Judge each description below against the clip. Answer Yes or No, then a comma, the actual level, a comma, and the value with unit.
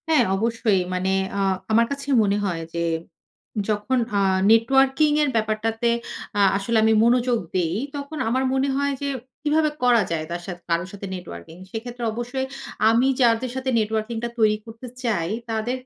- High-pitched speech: Yes, high, 225 Hz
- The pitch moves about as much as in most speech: Yes, average, 3.8 semitones